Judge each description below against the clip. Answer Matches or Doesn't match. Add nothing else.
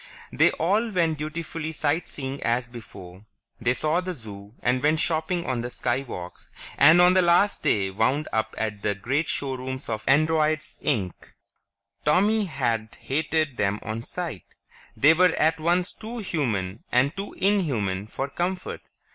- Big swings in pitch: Matches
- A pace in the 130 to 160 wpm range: Matches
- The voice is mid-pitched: Matches